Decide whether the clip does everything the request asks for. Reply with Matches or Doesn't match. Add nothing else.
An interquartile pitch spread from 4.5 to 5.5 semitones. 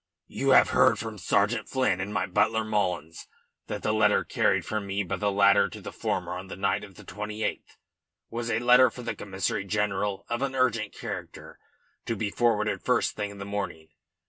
Doesn't match